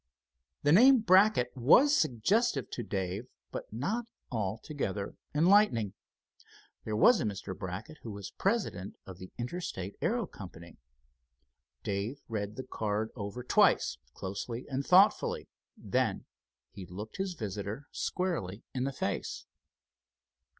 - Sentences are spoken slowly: Yes, slow, 120 wpm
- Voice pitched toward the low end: Yes, low, 115 Hz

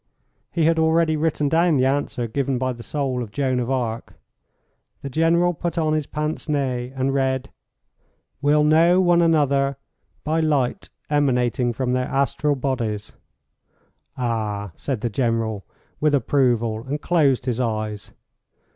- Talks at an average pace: Yes, average, 145 wpm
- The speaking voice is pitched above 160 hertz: No, low, 135 Hz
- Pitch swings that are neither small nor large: Yes, average, 3.9 semitones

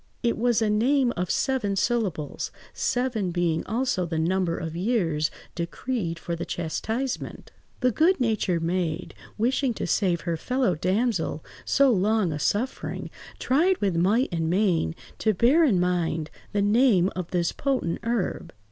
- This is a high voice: Yes, high, 200 Hz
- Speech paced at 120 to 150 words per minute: Yes, average, 145 wpm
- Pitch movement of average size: No, wide, 6.0 semitones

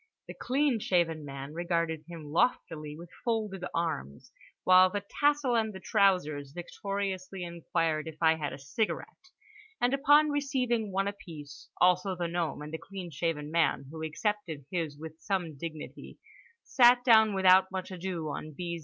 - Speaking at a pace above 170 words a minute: No, average, 155 wpm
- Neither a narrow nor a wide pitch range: Yes, average, 4.6 semitones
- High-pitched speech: No, medium, 180 Hz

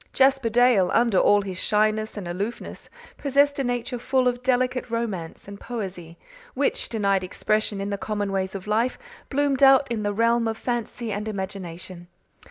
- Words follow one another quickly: No, average, 170 wpm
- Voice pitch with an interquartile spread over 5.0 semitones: No, average, 3.8 semitones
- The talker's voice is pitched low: No, high, 220 Hz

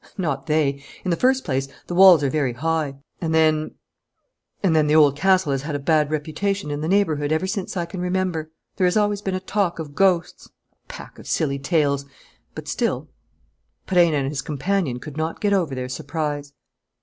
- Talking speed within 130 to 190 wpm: No, average, 200 wpm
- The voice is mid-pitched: Yes, medium, 160 Hz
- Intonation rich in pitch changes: No, average, 4.2 semitones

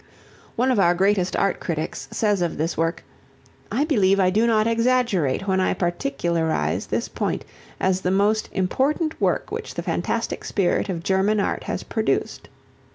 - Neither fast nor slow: Yes, average, 160 wpm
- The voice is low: No, high, 195 Hz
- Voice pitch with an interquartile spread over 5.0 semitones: No, average, 4.0 semitones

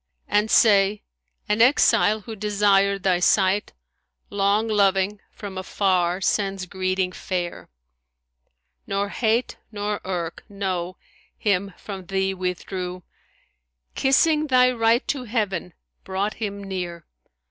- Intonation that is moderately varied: No, narrow, 2.2 semitones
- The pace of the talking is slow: Yes, slow, 115 wpm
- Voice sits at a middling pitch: No, high, 195 Hz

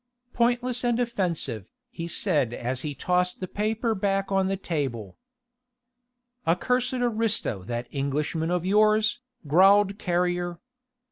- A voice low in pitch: No, medium, 185 Hz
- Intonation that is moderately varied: No, wide, 5.9 semitones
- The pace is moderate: No, slow, 125 wpm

